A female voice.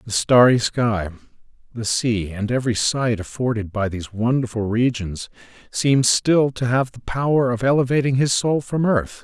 No: male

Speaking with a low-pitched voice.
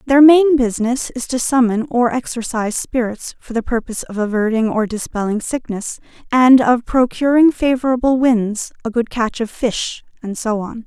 No: high, 240 Hz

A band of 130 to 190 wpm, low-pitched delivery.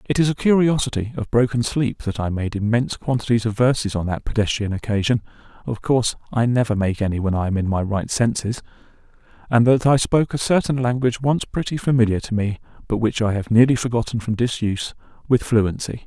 No: average, 200 wpm; low, 115 Hz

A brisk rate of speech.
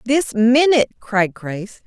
No: slow, 130 wpm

